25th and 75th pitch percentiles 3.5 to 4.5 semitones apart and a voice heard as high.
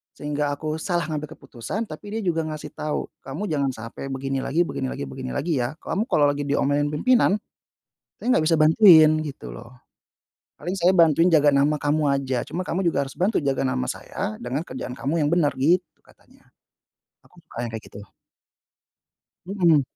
No: average, 3.8 semitones; medium, 150 Hz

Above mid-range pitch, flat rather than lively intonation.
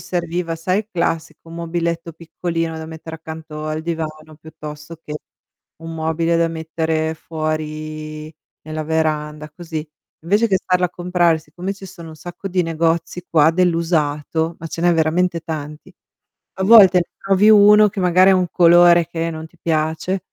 No: medium, 165 Hz; narrow, 1.9 semitones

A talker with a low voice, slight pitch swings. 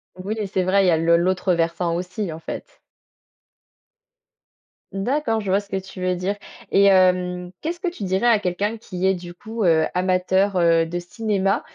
No: medium, 185 Hz; narrow, 2.2 semitones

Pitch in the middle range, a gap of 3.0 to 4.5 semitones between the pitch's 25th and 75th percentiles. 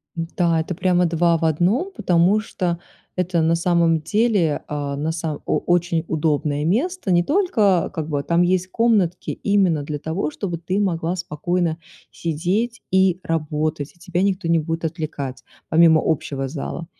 No: medium, 170 Hz; narrow, 2.6 semitones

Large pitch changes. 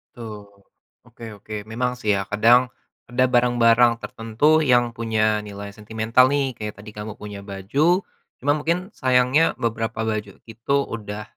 No: average, 2.9 semitones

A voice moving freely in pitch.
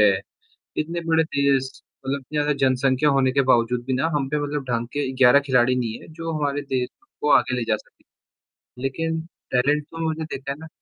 No: average, 2.7 semitones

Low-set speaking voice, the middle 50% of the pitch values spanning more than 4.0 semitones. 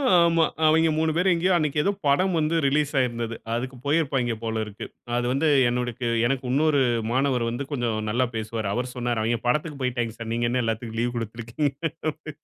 Yes: low, 125 Hz; average, 4.5 semitones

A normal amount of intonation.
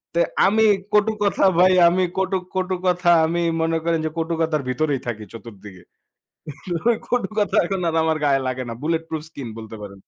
No: wide, 6.2 semitones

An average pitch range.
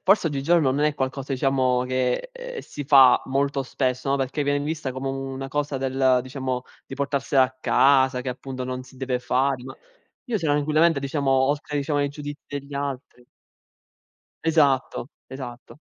No: narrow, 1.8 semitones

